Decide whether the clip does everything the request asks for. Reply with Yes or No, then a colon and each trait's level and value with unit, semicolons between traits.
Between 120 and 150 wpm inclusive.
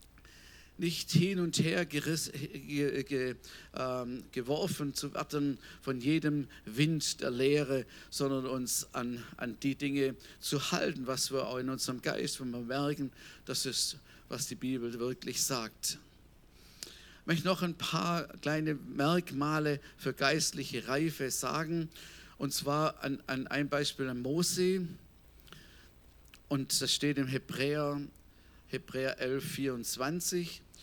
Yes: average, 130 wpm